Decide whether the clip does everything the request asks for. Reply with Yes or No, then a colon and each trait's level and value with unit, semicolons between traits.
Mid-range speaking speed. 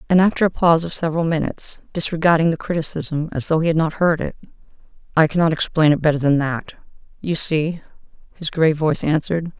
Yes: average, 180 wpm